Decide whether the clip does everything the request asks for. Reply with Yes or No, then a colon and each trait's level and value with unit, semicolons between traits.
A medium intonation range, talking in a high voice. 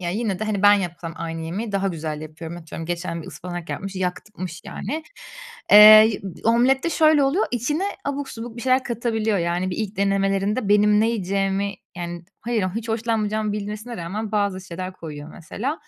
Yes: average, 4.2 semitones; high, 200 Hz